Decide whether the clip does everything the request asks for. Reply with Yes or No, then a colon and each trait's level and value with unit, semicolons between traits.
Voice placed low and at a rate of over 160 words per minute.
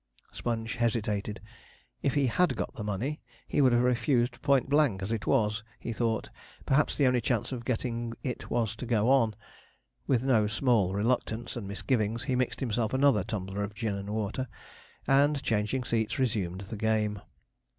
Yes: low, 115 Hz; average, 170 wpm